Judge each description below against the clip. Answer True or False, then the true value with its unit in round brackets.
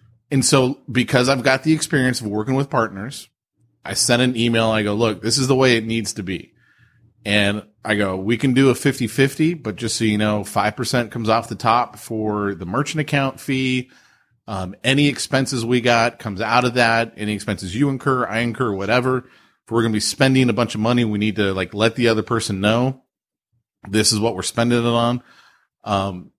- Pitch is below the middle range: True (115 Hz)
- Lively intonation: False (3.3 semitones)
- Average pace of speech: False (210 wpm)